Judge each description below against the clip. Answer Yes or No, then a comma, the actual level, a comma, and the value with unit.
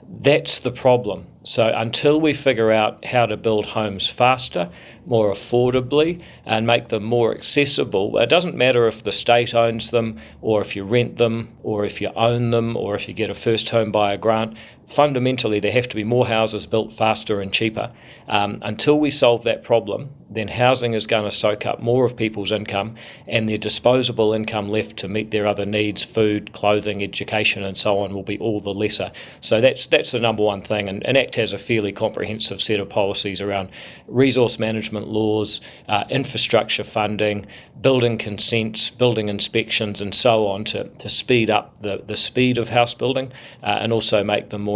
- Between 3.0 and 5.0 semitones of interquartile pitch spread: No, narrow, 2.4 semitones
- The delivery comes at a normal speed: Yes, average, 190 wpm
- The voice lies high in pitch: No, low, 110 Hz